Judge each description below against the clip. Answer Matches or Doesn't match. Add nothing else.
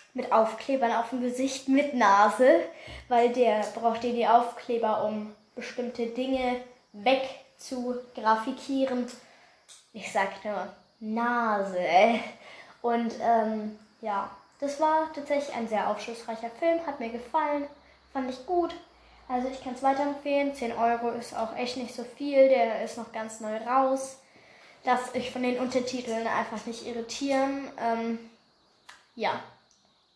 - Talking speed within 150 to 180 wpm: Doesn't match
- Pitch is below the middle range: Doesn't match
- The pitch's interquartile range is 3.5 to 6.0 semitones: Doesn't match